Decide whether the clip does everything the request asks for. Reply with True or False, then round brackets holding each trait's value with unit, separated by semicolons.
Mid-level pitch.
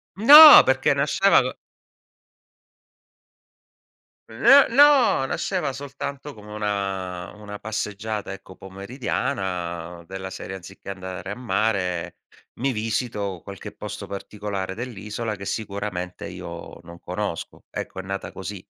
False (100 Hz)